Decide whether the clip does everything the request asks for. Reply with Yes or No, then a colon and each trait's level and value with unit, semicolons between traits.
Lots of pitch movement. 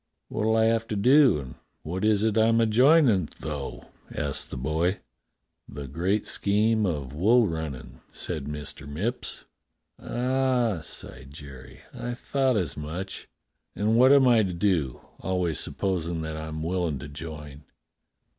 Yes: wide, 6.9 semitones